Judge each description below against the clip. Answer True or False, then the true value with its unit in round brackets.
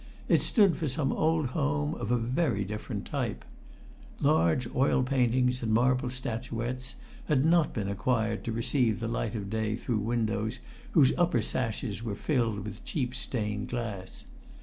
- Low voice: True (120 Hz)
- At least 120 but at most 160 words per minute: True (150 wpm)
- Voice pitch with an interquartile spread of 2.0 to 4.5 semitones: True (3.1 semitones)